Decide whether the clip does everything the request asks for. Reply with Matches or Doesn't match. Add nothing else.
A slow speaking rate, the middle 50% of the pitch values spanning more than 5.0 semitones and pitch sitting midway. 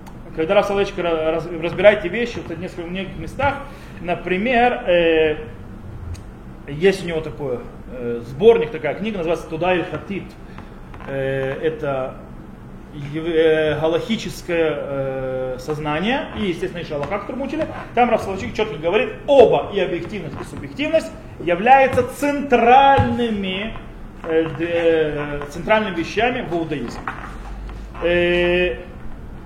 Matches